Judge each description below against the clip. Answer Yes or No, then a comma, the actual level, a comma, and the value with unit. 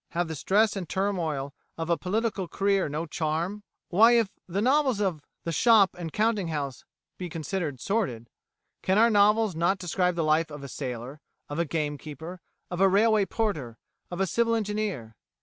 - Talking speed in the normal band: Yes, average, 175 wpm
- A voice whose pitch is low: No, medium, 180 Hz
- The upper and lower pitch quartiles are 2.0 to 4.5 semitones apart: No, average, 5.1 semitones